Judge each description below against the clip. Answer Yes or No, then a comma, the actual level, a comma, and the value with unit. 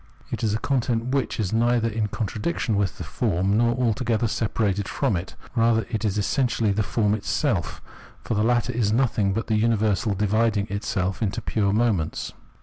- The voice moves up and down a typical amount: No, narrow, 2.3 semitones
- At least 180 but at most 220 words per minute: Yes, average, 185 wpm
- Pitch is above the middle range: No, low, 110 Hz